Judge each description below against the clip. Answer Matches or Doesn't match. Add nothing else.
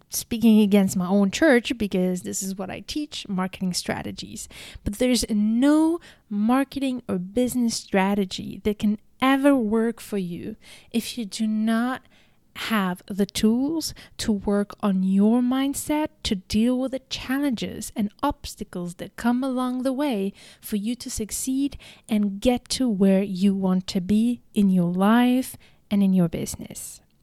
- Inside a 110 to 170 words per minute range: Matches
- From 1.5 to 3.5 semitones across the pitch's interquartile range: Doesn't match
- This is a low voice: Doesn't match